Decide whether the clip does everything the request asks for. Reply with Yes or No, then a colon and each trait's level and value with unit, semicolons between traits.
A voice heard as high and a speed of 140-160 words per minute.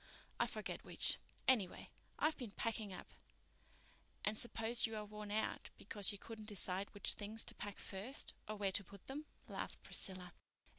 No: high, 210 Hz; average, 170 wpm